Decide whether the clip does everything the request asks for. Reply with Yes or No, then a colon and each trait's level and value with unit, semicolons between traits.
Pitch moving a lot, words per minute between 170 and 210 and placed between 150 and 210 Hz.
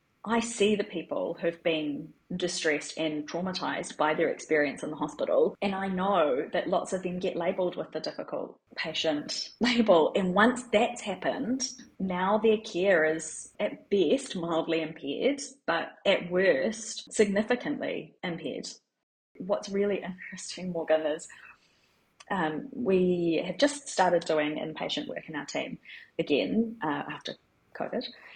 No: wide, 5.7 semitones; average, 140 wpm; high, 190 Hz